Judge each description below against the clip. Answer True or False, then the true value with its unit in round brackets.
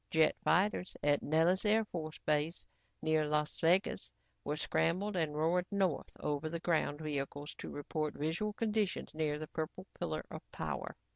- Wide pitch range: False (3.3 semitones)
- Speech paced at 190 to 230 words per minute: False (155 wpm)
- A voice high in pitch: False (160 Hz)